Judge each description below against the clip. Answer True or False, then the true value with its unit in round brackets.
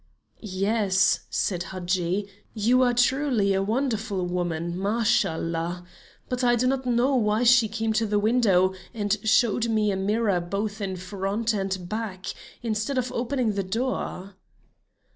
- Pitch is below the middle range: False (210 Hz)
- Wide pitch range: False (3.7 semitones)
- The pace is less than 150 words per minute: True (140 wpm)